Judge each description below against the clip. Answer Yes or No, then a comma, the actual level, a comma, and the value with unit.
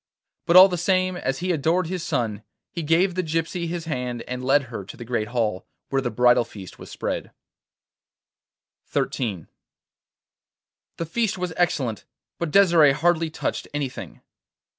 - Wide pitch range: Yes, wide, 6.2 semitones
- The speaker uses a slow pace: No, average, 155 wpm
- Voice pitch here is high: No, medium, 155 Hz